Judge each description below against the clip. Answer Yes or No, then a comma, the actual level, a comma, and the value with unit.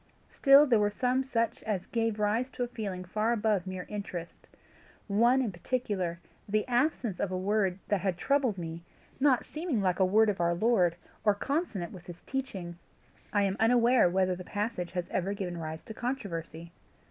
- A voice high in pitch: Yes, high, 205 Hz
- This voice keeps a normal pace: Yes, average, 180 wpm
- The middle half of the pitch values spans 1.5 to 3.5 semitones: No, average, 4.8 semitones